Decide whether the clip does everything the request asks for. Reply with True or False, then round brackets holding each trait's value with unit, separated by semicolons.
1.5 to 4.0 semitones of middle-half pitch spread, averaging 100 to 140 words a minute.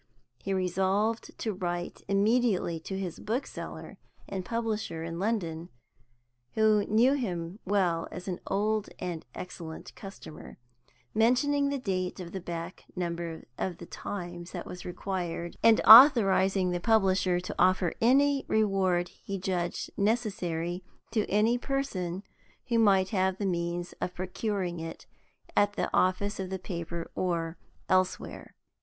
True (3.6 semitones; 135 wpm)